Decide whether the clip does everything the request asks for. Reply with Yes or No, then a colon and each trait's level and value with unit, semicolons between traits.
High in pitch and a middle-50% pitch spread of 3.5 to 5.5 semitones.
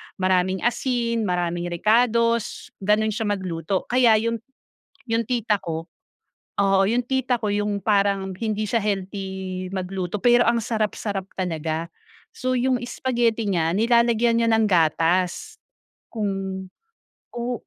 Yes: high, 210 Hz; average, 3.8 semitones